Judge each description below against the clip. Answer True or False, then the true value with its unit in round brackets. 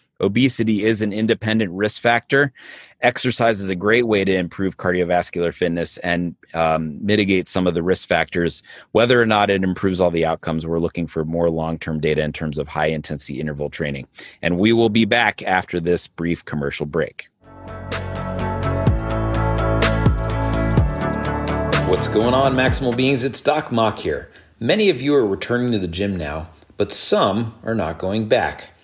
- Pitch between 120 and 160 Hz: False (95 Hz)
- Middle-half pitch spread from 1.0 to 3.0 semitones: False (5.0 semitones)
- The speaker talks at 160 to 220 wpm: True (165 wpm)